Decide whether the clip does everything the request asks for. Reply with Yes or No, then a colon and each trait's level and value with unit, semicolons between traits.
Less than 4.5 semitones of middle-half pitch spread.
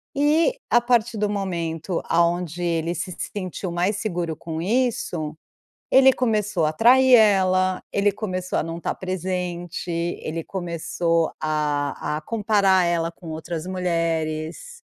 Yes: average, 3.8 semitones